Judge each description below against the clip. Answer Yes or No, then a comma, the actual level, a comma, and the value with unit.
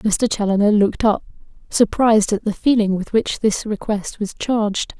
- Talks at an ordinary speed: Yes, average, 170 wpm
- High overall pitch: Yes, high, 215 Hz